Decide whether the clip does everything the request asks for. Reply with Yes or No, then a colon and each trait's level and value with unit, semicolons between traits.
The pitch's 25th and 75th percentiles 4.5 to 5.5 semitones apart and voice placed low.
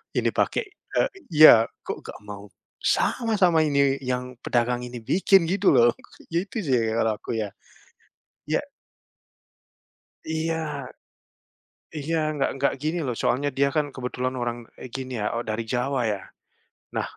Yes: average, 4.8 semitones; low, 130 Hz